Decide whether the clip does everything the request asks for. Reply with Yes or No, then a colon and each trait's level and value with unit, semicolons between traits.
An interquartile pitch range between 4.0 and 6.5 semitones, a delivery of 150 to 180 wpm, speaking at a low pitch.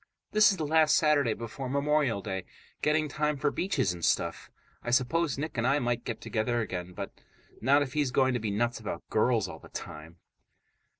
No: wide, 5.4 semitones; average, 195 wpm; low, 125 Hz